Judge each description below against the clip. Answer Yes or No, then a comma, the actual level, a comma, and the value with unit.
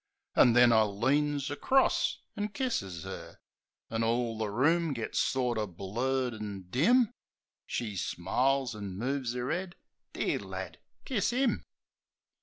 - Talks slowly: Yes, slow, 130 wpm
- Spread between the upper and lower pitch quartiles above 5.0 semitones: Yes, wide, 5.5 semitones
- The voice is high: No, low, 125 Hz